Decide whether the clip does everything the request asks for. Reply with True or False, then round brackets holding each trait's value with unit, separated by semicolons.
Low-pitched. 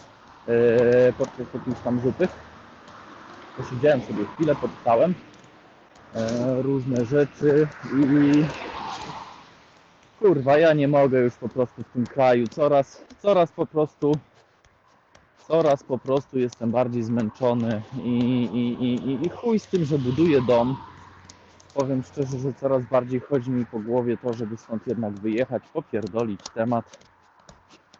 True (125 Hz)